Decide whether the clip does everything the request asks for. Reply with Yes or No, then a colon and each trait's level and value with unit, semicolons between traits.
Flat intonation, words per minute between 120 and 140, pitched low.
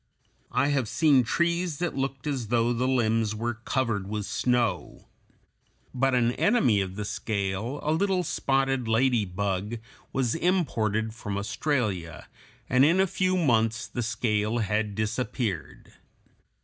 No: average, 4.1 semitones; slow, 135 wpm; low, 120 Hz